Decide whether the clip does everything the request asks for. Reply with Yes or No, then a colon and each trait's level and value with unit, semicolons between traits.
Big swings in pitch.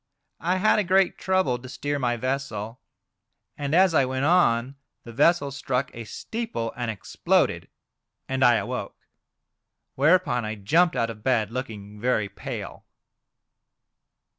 Yes: wide, 5.9 semitones